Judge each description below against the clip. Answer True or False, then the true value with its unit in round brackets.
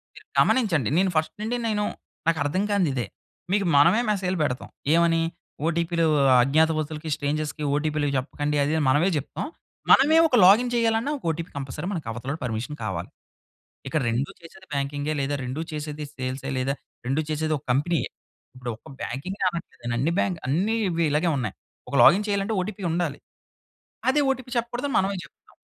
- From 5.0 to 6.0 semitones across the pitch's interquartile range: True (5.3 semitones)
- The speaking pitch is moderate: True (160 Hz)